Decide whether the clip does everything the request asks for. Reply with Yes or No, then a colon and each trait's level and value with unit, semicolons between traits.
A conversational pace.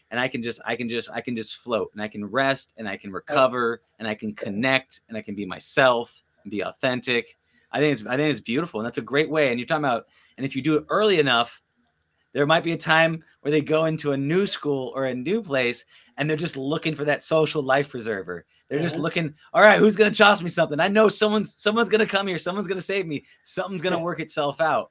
No: fast, 255 wpm